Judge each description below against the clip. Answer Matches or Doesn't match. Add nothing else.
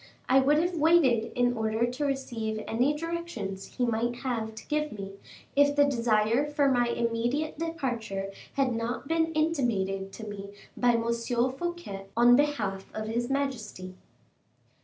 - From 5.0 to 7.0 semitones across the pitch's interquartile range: Doesn't match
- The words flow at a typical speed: Matches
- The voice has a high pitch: Matches